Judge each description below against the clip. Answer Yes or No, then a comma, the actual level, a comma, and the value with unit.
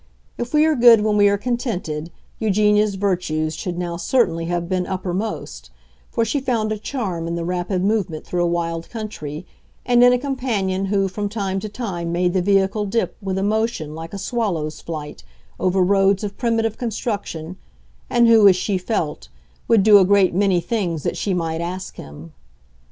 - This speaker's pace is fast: No, average, 185 wpm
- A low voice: No, high, 195 Hz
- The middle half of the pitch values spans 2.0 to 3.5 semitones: No, average, 4.0 semitones